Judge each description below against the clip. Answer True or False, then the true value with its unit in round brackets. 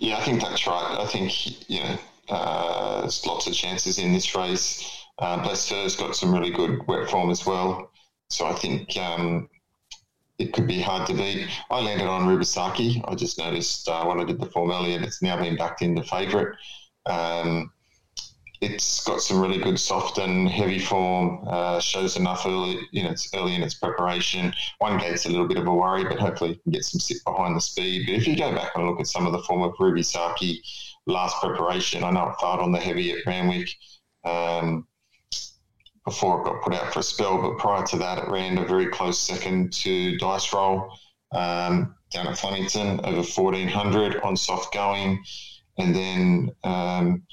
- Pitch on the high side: False (90 Hz)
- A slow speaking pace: False (200 wpm)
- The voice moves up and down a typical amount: False (2.1 semitones)